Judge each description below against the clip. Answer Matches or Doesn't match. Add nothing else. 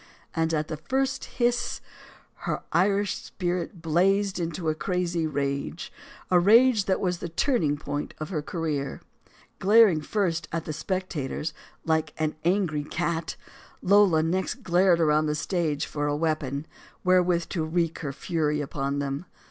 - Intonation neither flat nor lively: Matches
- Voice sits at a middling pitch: Matches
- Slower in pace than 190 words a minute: Matches